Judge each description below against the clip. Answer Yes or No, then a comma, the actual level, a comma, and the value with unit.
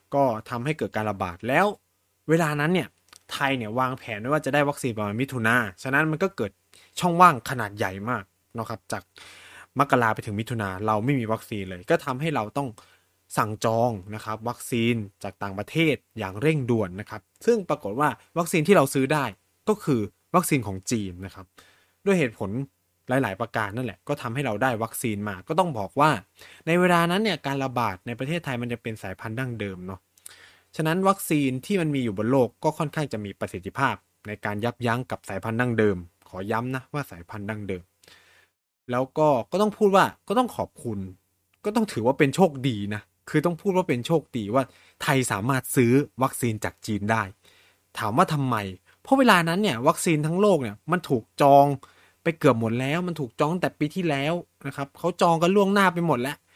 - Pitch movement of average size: No, wide, 6.4 semitones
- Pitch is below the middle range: Yes, low, 130 Hz